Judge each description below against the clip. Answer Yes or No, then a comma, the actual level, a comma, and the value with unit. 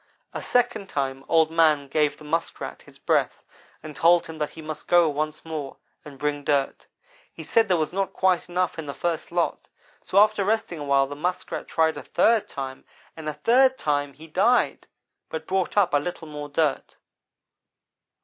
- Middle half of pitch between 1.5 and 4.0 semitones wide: Yes, average, 3.7 semitones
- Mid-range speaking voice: Yes, medium, 160 Hz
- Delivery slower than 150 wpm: No, average, 190 wpm